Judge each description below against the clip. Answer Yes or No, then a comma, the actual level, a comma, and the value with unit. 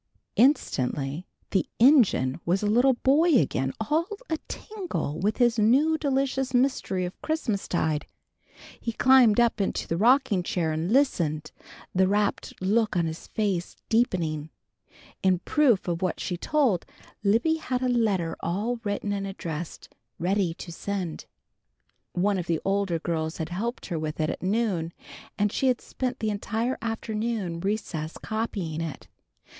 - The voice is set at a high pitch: Yes, high, 205 Hz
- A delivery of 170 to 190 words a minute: No, average, 150 wpm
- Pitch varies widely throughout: Yes, wide, 6.0 semitones